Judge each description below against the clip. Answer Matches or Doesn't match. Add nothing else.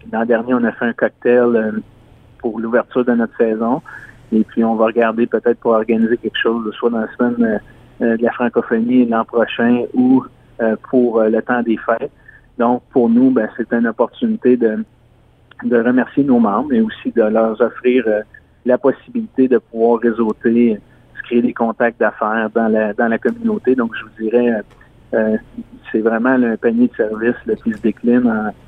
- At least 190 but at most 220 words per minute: Doesn't match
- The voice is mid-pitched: Doesn't match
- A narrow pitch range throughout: Matches